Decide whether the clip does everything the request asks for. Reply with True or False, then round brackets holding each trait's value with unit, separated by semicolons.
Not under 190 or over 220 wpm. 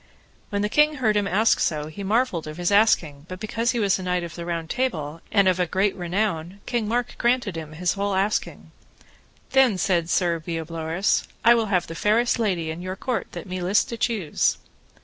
True (205 wpm)